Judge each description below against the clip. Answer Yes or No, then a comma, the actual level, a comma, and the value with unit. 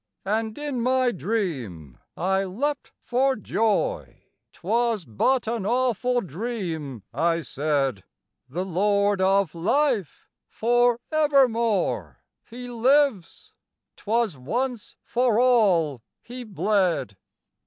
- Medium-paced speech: No, slow, 100 wpm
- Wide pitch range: Yes, wide, 6.0 semitones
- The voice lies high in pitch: Yes, high, 220 Hz